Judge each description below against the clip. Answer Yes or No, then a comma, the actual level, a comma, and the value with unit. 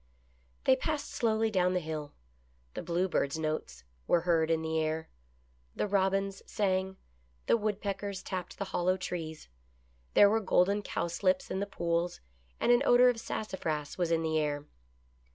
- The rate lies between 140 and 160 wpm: Yes, average, 150 wpm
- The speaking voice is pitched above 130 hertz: Yes, medium, 185 Hz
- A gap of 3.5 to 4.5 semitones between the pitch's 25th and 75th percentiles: Yes, average, 3.9 semitones